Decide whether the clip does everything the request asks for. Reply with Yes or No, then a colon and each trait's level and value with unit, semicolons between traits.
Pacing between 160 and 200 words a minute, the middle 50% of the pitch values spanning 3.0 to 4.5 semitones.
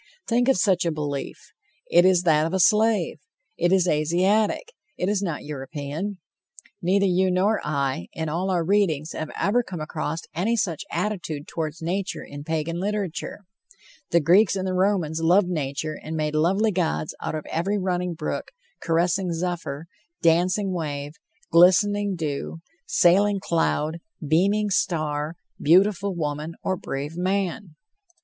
No: average, 145 wpm; average, 3.8 semitones